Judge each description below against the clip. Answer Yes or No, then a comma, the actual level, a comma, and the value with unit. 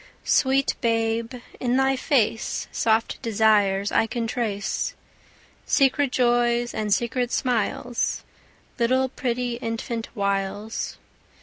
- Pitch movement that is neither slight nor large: No, narrow, 2.2 semitones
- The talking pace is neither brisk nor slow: No, slow, 100 wpm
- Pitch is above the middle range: Yes, high, 235 Hz